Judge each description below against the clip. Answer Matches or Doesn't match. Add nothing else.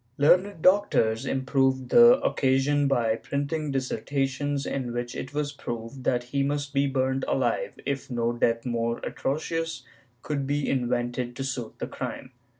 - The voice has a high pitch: Doesn't match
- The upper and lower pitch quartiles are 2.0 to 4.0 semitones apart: Matches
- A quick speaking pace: Doesn't match